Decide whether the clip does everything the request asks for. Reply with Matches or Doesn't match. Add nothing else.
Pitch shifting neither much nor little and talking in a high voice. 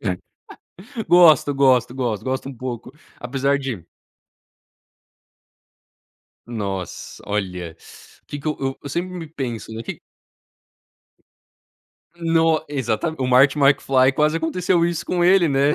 Doesn't match